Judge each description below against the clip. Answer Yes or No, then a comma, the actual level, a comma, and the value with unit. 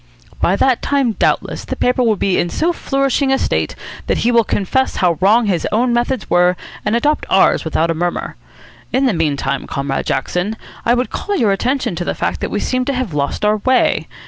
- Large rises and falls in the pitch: Yes, wide, 6.5 semitones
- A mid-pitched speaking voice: No, high, 220 Hz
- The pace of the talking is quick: Yes, fast, 210 wpm